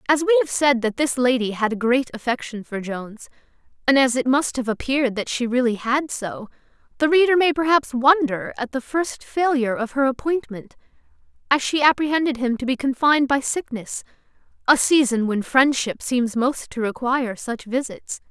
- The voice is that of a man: No, female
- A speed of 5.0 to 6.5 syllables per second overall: Yes, 5.3 syllables/s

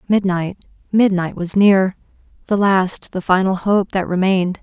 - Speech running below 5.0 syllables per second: Yes, 4.5 syllables/s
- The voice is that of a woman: Yes, female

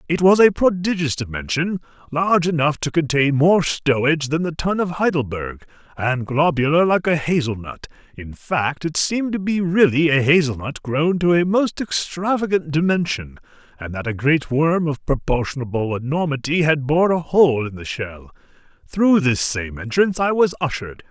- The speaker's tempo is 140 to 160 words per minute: No, average, 170 wpm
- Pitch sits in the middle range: Yes, medium, 155 Hz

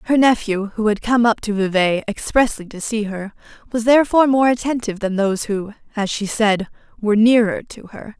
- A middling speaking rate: Yes, average, 190 wpm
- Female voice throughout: Yes, female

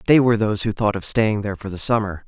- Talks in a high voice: No, low, 105 Hz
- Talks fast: Yes, fast, 290 wpm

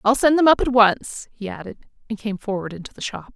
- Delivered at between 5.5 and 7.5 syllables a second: Yes, 5.9 syllables/s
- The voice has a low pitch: No, high, 225 Hz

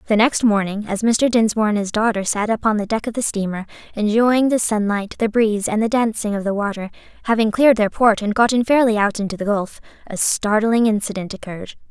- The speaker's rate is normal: No, fast, 210 wpm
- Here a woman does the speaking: Yes, female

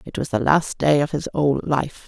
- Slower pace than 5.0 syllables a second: Yes, 4.7 syllables/s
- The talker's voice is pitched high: No, medium, 145 Hz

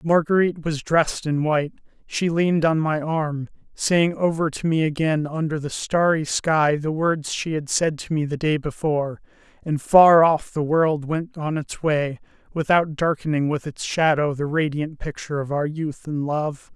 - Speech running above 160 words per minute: Yes, average, 185 wpm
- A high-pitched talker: No, medium, 155 Hz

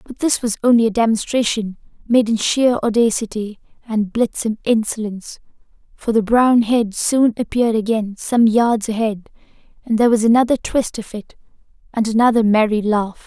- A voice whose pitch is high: Yes, high, 225 Hz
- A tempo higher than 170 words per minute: No, average, 155 wpm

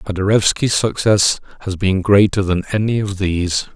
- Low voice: Yes, low, 100 Hz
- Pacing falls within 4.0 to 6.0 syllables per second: Yes, 5.2 syllables/s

